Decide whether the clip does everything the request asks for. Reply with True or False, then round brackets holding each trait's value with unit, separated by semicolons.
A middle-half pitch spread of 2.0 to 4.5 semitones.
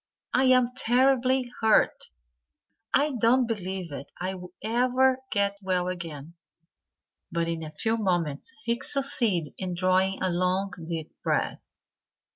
False (5.6 semitones)